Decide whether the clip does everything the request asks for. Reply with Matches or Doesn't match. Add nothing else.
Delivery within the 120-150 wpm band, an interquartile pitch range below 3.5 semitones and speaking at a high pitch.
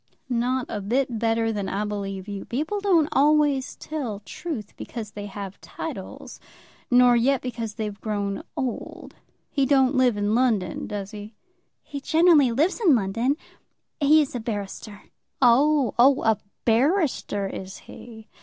Doesn't match